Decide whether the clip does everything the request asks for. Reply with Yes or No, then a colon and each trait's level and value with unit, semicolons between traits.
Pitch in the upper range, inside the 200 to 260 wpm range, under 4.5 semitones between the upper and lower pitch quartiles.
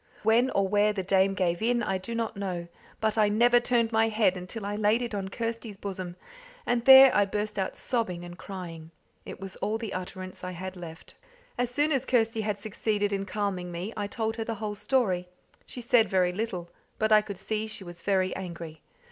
Yes: high, 205 Hz; fast, 205 wpm; average, 3.2 semitones